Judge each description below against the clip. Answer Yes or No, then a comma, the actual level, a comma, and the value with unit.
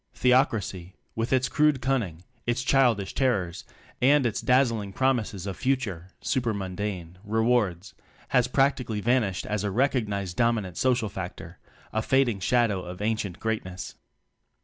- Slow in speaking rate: Yes, slow, 130 wpm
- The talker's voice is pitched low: Yes, low, 110 Hz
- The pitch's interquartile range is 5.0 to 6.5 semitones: No, average, 4.6 semitones